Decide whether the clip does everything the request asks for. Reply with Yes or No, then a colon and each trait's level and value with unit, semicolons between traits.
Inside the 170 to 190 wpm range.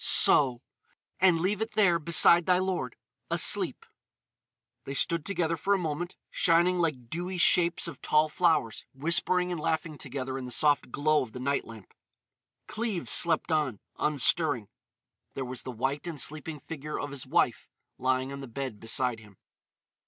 No: average, 160 wpm